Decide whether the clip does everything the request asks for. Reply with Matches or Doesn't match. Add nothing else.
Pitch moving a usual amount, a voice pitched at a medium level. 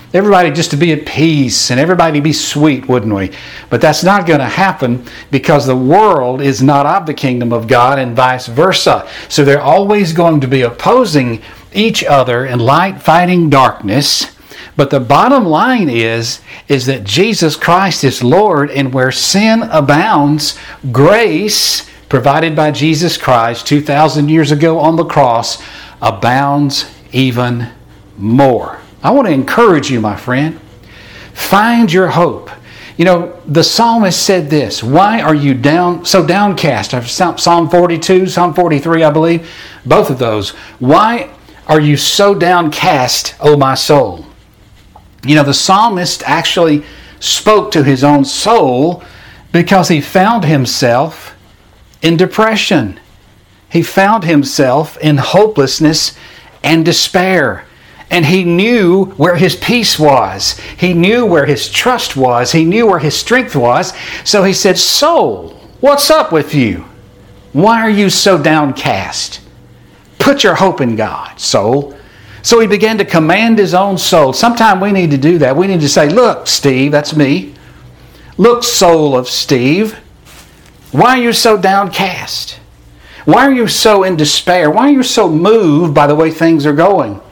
Doesn't match